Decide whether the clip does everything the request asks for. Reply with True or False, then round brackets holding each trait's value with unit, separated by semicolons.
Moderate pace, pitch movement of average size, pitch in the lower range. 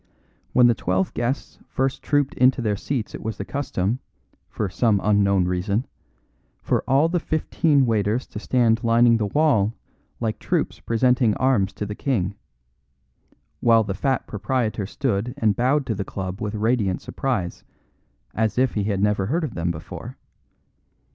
True (160 wpm; 4.2 semitones; 115 Hz)